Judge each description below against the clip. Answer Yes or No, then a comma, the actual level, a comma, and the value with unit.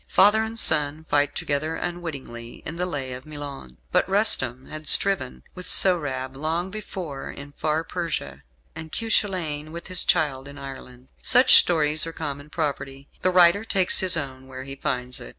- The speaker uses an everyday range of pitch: Yes, average, 4.5 semitones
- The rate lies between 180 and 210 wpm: No, average, 170 wpm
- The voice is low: No, medium, 150 Hz